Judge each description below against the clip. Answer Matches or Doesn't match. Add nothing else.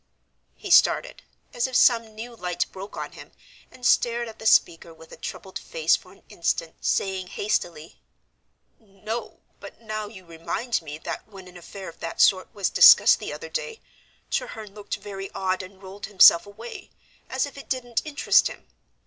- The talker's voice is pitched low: Doesn't match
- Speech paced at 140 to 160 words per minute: Doesn't match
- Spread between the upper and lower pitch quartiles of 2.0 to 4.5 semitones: Matches